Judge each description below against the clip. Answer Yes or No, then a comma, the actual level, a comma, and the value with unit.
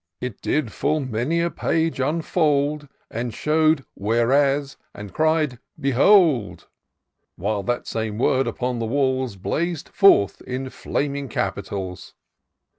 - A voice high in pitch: No, low, 135 Hz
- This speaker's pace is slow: Yes, slow, 130 wpm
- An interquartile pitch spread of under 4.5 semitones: No, average, 4.9 semitones